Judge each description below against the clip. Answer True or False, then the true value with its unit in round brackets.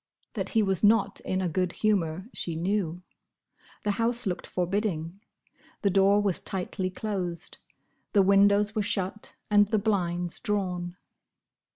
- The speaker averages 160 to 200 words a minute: False (140 wpm)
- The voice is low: False (195 Hz)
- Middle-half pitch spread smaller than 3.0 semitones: True (2.6 semitones)